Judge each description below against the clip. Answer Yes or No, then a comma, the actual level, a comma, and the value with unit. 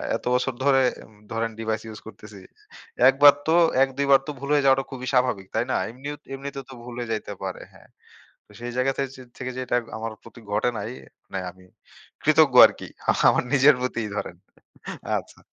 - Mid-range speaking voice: No, low, 125 Hz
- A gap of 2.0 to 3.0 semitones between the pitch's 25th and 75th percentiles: No, average, 3.5 semitones